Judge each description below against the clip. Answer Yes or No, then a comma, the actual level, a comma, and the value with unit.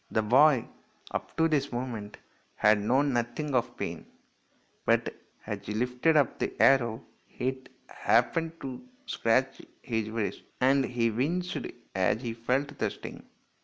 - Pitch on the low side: Yes, low, 125 Hz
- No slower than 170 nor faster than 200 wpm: No, average, 140 wpm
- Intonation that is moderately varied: Yes, average, 3.7 semitones